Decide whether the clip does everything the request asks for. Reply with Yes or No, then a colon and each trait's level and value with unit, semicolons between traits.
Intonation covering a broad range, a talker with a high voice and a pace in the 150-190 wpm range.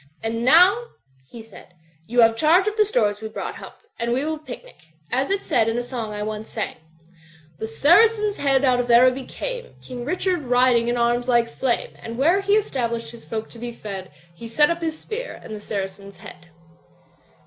No: wide, 6.1 semitones; high, 245 Hz; average, 200 wpm